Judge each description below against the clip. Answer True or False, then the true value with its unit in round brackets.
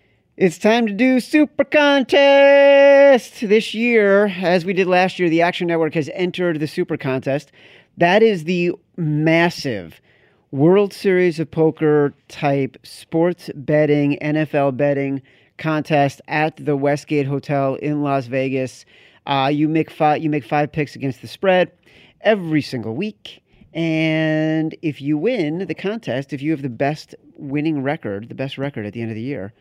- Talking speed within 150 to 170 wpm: True (160 wpm)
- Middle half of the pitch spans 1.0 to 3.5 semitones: False (4.3 semitones)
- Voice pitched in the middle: True (155 Hz)